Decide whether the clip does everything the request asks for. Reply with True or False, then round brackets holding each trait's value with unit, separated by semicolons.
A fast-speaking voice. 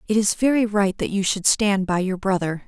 True (245 wpm)